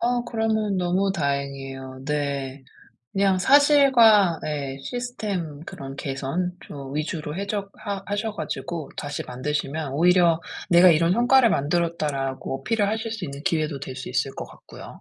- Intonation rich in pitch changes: Yes, wide, 6.5 semitones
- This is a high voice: No, medium, 165 Hz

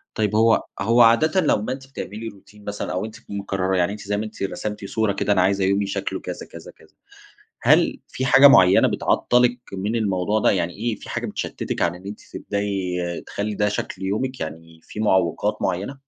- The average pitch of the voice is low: Yes, low, 105 Hz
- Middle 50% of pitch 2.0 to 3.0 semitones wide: Yes, average, 2.7 semitones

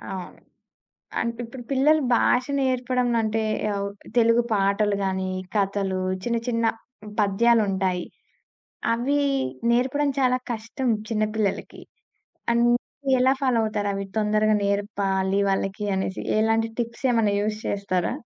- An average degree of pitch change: Yes, average, 3.3 semitones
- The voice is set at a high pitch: Yes, high, 220 Hz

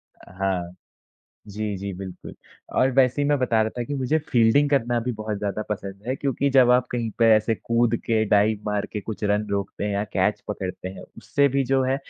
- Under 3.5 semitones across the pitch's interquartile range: No, average, 3.8 semitones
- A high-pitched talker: No, low, 110 Hz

